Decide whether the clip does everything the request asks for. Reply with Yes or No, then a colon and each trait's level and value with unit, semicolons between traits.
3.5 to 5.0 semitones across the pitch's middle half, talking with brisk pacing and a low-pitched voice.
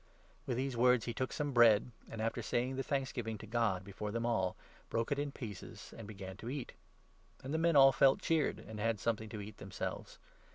Yes: average, 3.8 semitones; fast, 220 wpm; low, 115 Hz